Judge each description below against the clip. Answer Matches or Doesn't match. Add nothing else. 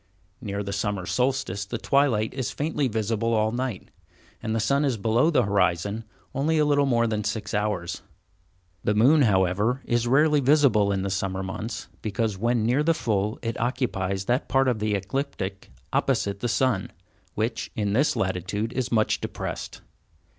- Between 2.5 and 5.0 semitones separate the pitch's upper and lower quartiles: Matches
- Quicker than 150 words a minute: Matches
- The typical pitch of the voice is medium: Doesn't match